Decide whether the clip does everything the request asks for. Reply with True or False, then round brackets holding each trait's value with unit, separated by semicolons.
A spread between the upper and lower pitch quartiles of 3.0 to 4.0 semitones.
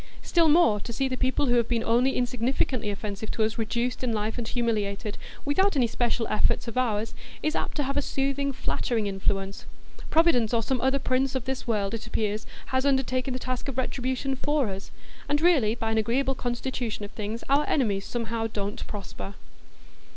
True (3.4 semitones)